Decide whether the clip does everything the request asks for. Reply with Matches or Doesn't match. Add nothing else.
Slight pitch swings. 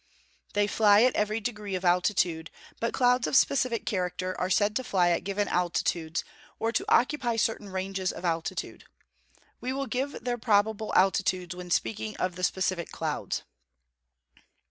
Doesn't match